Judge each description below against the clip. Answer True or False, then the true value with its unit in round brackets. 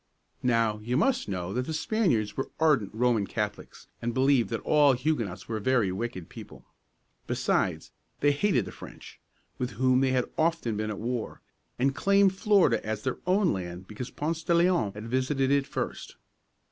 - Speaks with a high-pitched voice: False (125 Hz)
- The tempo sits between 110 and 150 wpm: False (170 wpm)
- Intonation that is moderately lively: False (5.8 semitones)